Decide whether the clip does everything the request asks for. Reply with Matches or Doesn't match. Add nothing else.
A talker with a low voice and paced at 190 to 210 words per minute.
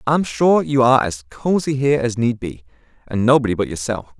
Matches